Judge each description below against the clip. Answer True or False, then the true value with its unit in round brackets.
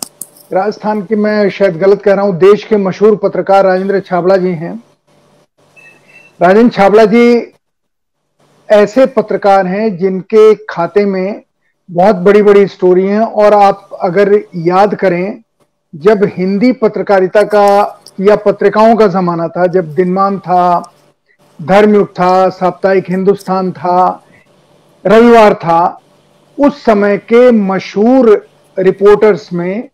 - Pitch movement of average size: False (2.2 semitones)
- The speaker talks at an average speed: True (120 wpm)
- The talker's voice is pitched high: True (195 Hz)